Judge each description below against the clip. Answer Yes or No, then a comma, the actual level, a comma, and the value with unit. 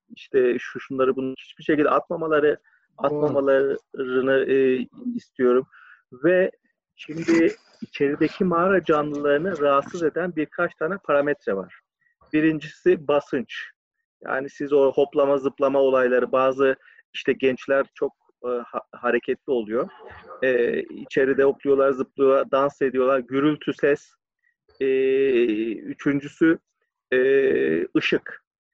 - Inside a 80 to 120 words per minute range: Yes, average, 100 wpm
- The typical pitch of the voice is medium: Yes, medium, 150 Hz